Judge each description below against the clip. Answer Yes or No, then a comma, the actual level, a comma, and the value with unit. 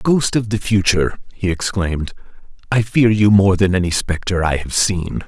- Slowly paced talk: No, average, 180 wpm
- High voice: No, very low, 95 Hz